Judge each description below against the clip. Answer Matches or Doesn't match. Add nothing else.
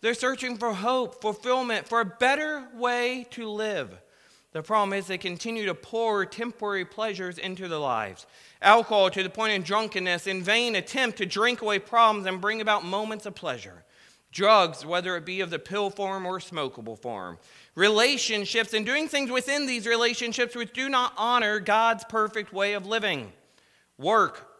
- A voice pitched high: Matches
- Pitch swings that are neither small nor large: Matches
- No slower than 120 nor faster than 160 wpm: Doesn't match